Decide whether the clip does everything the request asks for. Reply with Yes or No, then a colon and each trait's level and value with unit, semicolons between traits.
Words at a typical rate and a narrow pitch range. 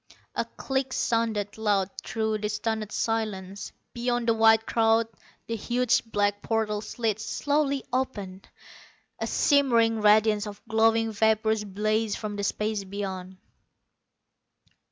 No: slow, 120 wpm; narrow, 1.7 semitones